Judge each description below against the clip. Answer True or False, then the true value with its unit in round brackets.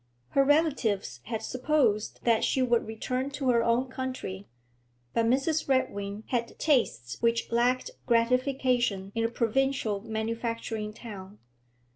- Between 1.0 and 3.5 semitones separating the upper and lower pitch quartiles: True (3.1 semitones)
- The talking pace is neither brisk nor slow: False (125 wpm)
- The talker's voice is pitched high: True (235 Hz)